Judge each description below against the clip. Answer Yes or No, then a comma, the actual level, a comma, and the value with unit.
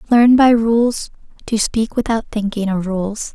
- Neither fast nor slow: Yes, average, 160 wpm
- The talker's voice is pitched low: No, high, 220 Hz